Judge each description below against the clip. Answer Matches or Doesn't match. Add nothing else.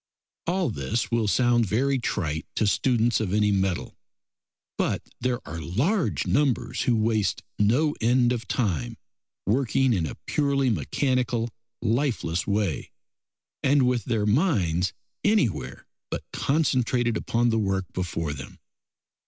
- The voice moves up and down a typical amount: Matches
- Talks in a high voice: Doesn't match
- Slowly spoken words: Matches